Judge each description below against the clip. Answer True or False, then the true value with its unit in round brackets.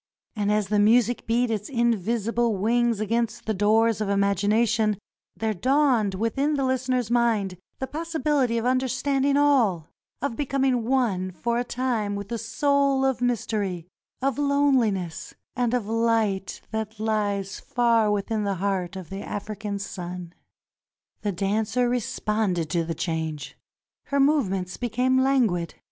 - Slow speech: False (145 wpm)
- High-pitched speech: True (225 Hz)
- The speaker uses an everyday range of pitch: True (3.9 semitones)